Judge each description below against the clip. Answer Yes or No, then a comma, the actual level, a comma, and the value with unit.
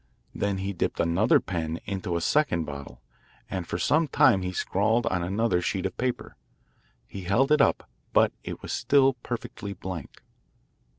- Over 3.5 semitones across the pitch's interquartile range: Yes, average, 5.2 semitones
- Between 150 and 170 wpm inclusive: Yes, average, 165 wpm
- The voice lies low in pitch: Yes, very low, 95 Hz